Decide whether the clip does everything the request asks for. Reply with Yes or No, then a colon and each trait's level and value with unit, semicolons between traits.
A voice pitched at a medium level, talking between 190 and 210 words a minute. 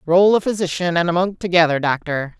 Yes: medium, 175 Hz; average, 200 wpm